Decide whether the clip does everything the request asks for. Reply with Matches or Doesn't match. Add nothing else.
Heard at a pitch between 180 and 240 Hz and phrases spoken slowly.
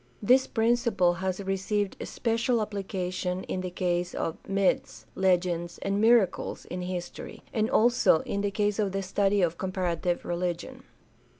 Doesn't match